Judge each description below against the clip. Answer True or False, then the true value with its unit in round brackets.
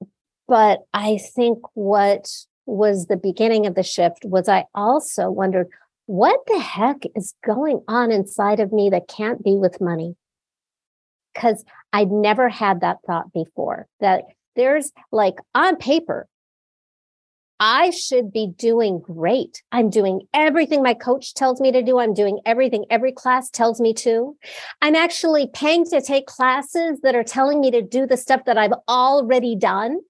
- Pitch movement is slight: False (4.5 semitones)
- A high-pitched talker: True (235 Hz)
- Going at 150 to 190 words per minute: True (160 wpm)